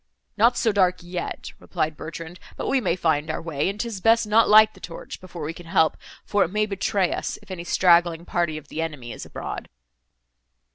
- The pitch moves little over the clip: No, average, 4.1 semitones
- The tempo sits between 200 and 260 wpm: Yes, fast, 205 wpm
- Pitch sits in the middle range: Yes, medium, 175 Hz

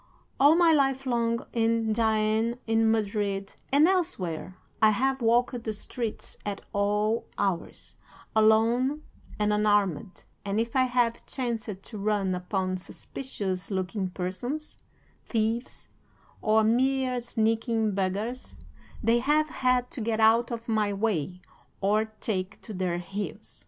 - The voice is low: No, high, 220 Hz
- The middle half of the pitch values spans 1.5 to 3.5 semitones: Yes, average, 3.1 semitones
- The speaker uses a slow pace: Yes, slow, 130 wpm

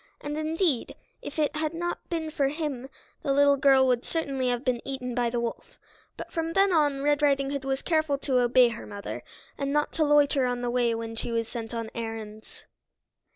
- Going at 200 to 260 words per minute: Yes, fast, 205 wpm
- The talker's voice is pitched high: Yes, very high, 275 Hz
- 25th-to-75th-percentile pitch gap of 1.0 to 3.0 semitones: No, average, 3.6 semitones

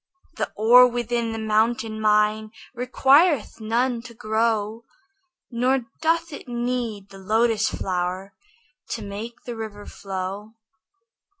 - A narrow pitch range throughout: Yes, narrow, 2.3 semitones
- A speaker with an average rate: No, slow, 115 wpm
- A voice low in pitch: No, high, 225 Hz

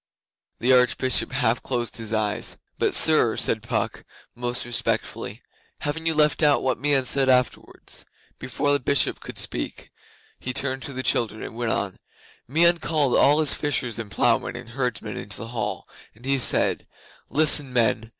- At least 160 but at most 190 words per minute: Yes, average, 170 wpm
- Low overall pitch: Yes, low, 130 Hz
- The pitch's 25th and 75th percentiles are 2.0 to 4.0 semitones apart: Yes, average, 3.4 semitones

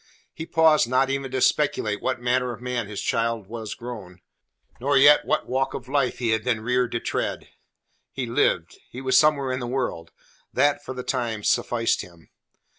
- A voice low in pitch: Yes, low, 125 Hz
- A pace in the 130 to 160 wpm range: No, average, 190 wpm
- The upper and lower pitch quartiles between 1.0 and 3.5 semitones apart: Yes, average, 2.7 semitones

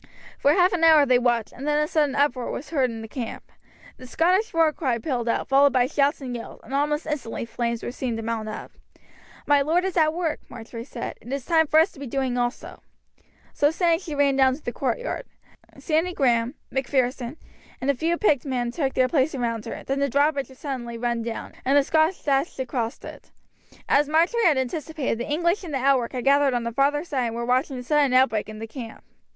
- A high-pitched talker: Yes, very high, 275 Hz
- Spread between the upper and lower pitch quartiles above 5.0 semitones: No, average, 3.9 semitones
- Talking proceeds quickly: Yes, fast, 225 wpm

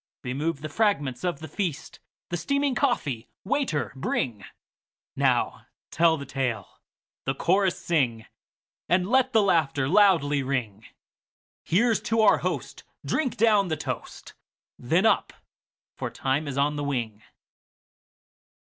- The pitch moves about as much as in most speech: No, wide, 7.0 semitones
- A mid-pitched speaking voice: Yes, medium, 155 Hz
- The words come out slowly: Yes, slow, 115 wpm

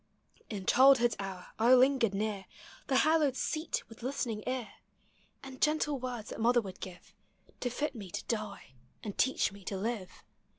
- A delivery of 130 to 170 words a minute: Yes, average, 165 wpm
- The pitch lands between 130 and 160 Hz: No, high, 235 Hz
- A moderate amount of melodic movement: Yes, average, 4.5 semitones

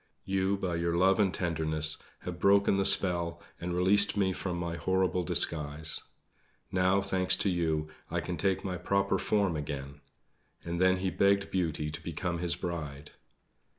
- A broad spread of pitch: No, narrow, 2.5 semitones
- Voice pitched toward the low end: Yes, very low, 90 Hz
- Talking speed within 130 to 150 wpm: No, average, 160 wpm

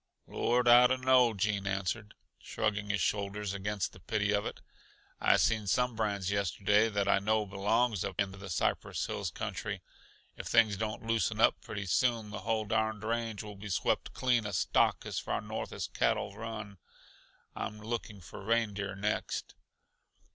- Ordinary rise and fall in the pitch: No, narrow, 2.2 semitones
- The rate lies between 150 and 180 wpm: Yes, average, 165 wpm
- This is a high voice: No, low, 105 Hz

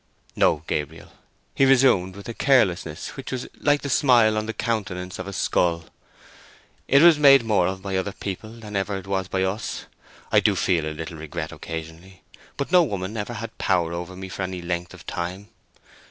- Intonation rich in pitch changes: No, average, 4.5 semitones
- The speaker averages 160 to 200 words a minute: Yes, average, 195 wpm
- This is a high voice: No, very low, 95 Hz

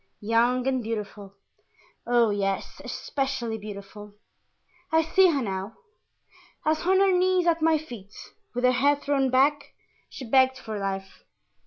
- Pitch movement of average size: No, wide, 5.7 semitones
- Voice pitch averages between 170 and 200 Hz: No, very high, 250 Hz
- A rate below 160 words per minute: Yes, average, 140 wpm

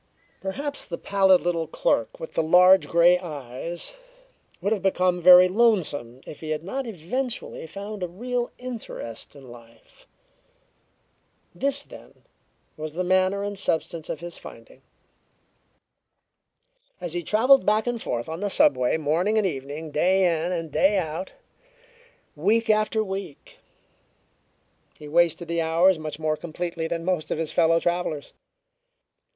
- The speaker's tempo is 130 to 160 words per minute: Yes, average, 140 wpm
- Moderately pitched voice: Yes, medium, 175 Hz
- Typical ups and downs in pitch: Yes, average, 4.0 semitones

